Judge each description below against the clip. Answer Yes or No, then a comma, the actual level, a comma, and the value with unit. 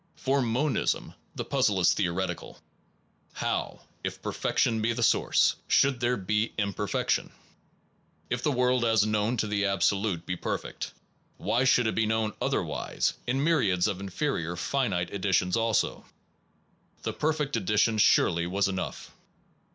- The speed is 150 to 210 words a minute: No, average, 140 wpm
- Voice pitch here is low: Yes, low, 110 Hz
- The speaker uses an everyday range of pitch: Yes, average, 4.2 semitones